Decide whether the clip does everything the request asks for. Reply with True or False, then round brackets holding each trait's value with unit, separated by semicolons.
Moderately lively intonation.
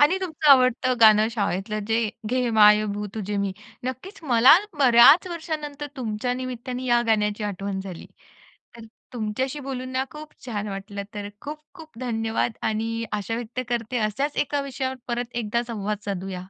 True (3.8 semitones)